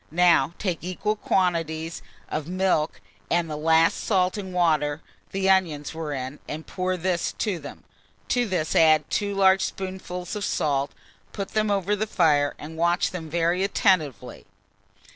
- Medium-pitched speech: Yes, medium, 175 Hz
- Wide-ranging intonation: No, average, 3.3 semitones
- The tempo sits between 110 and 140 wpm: No, average, 155 wpm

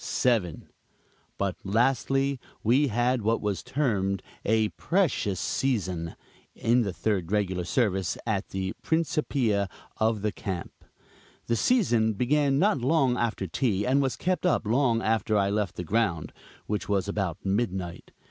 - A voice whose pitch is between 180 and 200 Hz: No, low, 110 Hz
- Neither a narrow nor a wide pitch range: Yes, average, 4.7 semitones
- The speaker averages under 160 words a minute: Yes, average, 140 wpm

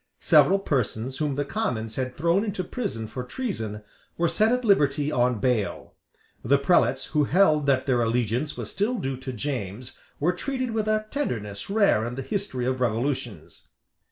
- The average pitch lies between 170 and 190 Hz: No, medium, 140 Hz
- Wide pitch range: Yes, wide, 8.1 semitones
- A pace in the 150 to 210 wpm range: Yes, average, 170 wpm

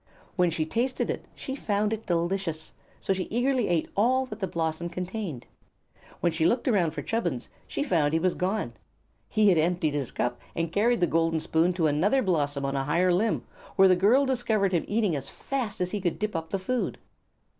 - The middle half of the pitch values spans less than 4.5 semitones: No, average, 4.9 semitones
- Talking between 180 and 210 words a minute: Yes, fast, 205 wpm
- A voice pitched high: No, medium, 180 Hz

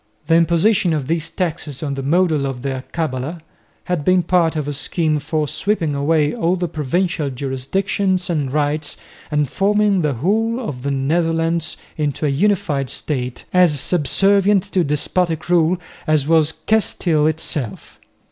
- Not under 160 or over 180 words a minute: No, average, 150 wpm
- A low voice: No, medium, 160 Hz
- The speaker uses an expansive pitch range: No, average, 3.7 semitones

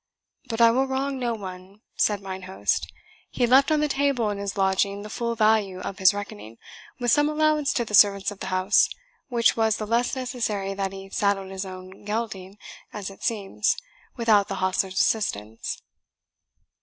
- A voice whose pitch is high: Yes, high, 205 Hz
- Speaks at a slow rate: No, average, 180 wpm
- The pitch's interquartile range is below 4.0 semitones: Yes, average, 3.5 semitones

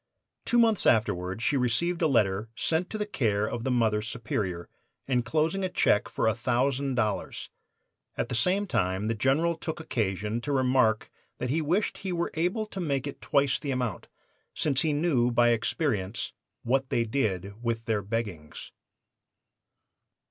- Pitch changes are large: Yes, wide, 6.0 semitones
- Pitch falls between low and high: No, low, 125 Hz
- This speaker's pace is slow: No, average, 160 wpm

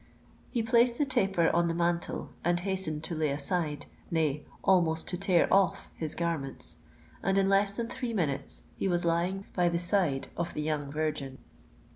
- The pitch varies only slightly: No, average, 3.8 semitones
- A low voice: No, medium, 170 Hz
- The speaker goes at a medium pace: Yes, average, 170 wpm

